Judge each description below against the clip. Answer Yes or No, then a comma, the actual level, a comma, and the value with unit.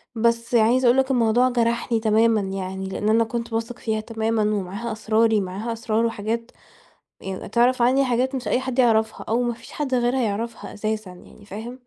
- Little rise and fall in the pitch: Yes, narrow, 1.9 semitones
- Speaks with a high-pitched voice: Yes, high, 230 Hz